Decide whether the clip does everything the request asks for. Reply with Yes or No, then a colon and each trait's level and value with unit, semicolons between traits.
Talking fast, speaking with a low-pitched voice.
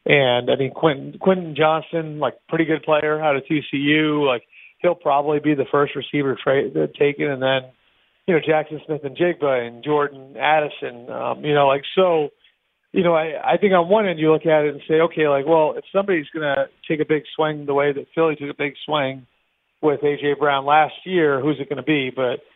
No: fast, 210 wpm; medium, 150 Hz